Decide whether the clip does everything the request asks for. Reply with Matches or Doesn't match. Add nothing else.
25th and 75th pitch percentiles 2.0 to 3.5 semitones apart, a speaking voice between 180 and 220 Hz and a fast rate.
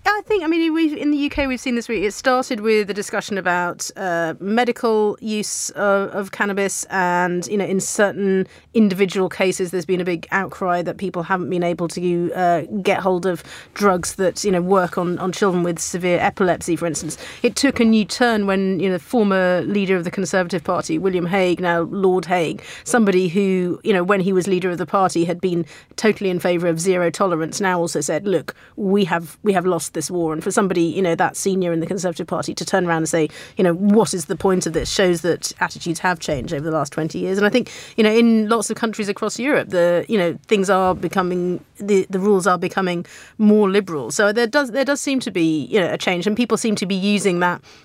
Matches